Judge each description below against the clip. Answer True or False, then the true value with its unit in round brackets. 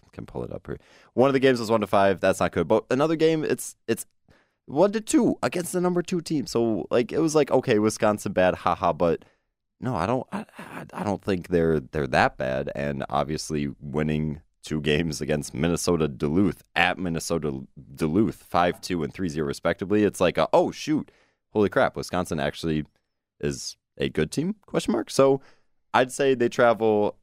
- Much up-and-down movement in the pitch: True (8.8 semitones)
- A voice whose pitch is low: True (95 Hz)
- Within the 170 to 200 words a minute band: True (190 wpm)